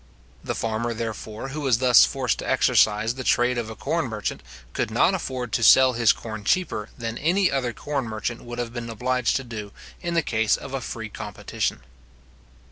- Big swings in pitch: No, average, 2.7 semitones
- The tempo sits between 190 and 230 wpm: Yes, average, 195 wpm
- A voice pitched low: Yes, low, 120 Hz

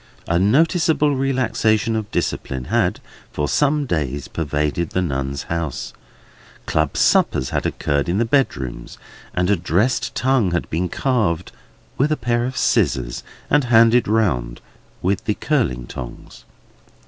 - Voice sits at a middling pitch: No, low, 100 Hz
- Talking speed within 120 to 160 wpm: Yes, average, 140 wpm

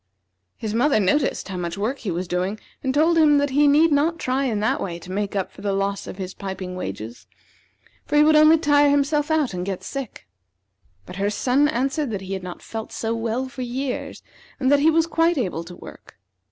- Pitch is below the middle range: No, high, 245 Hz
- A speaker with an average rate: No, fast, 220 wpm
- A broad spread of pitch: Yes, wide, 7.0 semitones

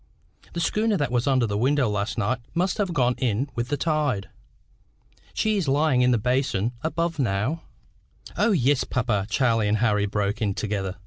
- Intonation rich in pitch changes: Yes, wide, 6.0 semitones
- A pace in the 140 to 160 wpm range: No, average, 180 wpm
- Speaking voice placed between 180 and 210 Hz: No, low, 125 Hz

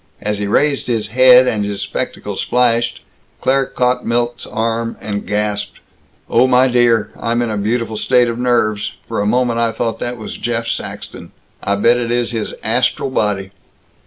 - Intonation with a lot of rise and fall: No, narrow, 2.6 semitones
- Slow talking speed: No, average, 175 wpm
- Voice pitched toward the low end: Yes, low, 115 Hz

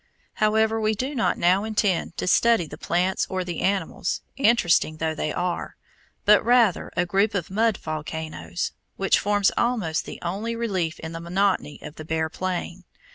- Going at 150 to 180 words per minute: Yes, average, 170 wpm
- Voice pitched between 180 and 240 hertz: Yes, medium, 185 Hz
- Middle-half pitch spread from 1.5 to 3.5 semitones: No, average, 4.5 semitones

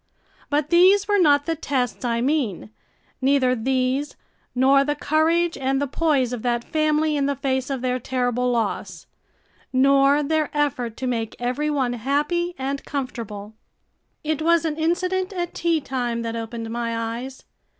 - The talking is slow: No, average, 160 wpm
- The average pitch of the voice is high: Yes, very high, 275 Hz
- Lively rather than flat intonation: No, average, 3.9 semitones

